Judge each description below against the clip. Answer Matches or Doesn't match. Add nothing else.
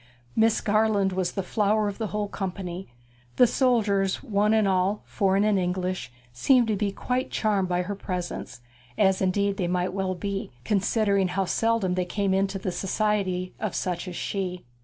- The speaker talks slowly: Doesn't match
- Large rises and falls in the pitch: Doesn't match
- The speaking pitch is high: Matches